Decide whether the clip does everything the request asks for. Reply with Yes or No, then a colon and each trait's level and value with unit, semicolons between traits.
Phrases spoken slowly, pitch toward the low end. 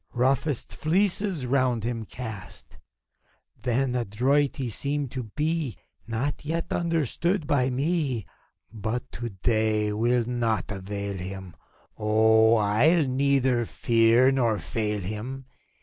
Yes: slow, 120 wpm; low, 120 Hz